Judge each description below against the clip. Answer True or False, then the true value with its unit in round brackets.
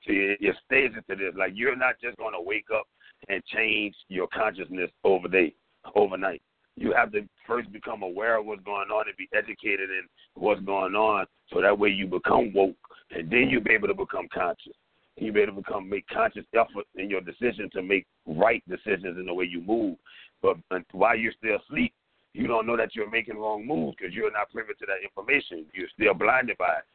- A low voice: True (110 Hz)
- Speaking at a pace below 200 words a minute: False (205 wpm)